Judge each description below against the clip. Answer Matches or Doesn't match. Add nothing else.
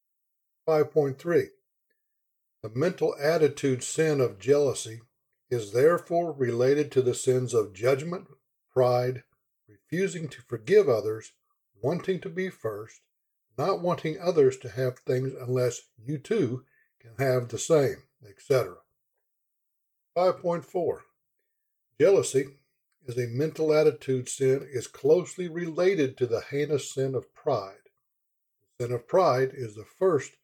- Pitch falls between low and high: Matches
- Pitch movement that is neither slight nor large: Doesn't match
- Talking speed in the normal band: Doesn't match